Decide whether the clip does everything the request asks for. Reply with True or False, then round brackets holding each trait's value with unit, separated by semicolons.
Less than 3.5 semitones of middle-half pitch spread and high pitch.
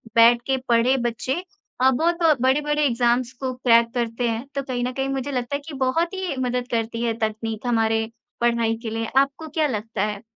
True (2.9 semitones; 245 Hz)